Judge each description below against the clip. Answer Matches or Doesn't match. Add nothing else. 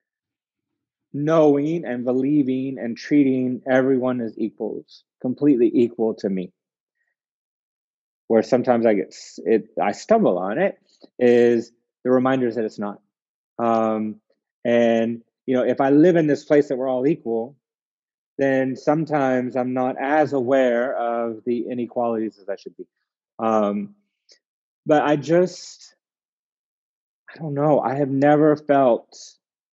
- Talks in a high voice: Doesn't match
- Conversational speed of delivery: Doesn't match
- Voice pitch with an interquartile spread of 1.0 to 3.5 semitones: Doesn't match